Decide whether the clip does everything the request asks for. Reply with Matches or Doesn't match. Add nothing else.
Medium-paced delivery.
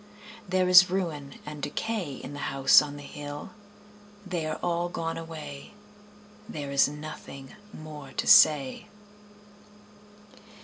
Doesn't match